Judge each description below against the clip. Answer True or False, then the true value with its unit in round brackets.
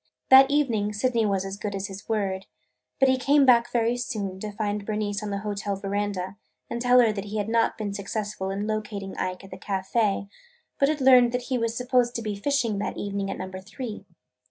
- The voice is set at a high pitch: True (210 Hz)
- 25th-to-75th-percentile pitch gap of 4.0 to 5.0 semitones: False (3.2 semitones)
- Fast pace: True (215 wpm)